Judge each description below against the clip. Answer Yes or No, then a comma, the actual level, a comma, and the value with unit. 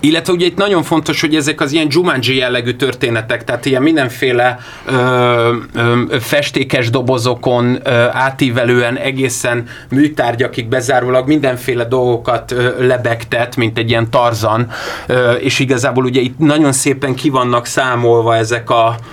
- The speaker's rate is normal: Yes, average, 130 wpm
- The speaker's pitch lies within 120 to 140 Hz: Yes, low, 125 Hz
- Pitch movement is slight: Yes, narrow, 2.3 semitones